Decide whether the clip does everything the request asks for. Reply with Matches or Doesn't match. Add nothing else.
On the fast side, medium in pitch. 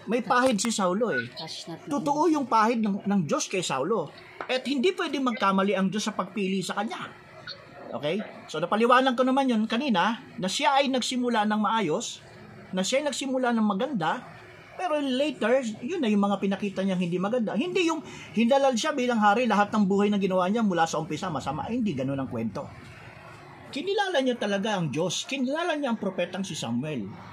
Doesn't match